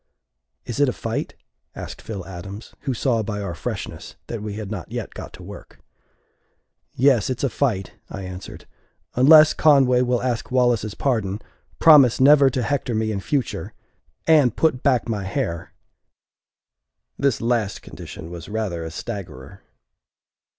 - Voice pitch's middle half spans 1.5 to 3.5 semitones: No, average, 4.9 semitones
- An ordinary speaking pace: Yes, average, 150 wpm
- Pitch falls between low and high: No, low, 115 Hz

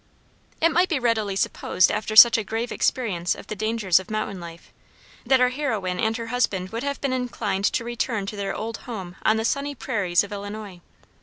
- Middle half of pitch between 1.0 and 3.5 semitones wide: No, average, 3.9 semitones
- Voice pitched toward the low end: No, high, 220 Hz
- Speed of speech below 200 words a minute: No, fast, 205 wpm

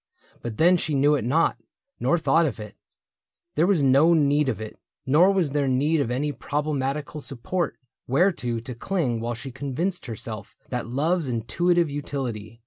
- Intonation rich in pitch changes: No, average, 4.8 semitones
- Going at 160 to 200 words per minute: Yes, average, 165 wpm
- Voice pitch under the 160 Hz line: Yes, medium, 140 Hz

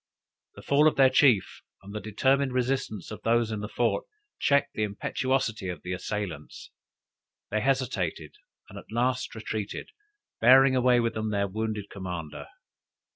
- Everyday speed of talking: Yes, average, 150 wpm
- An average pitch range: Yes, average, 4.3 semitones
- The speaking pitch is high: No, low, 110 Hz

